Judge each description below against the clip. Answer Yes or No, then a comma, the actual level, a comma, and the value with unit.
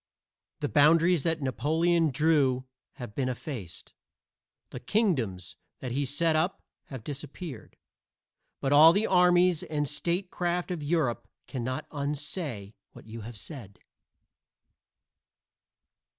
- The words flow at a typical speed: No, slow, 110 wpm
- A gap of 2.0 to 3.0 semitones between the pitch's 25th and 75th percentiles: No, average, 4.7 semitones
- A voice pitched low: No, medium, 150 Hz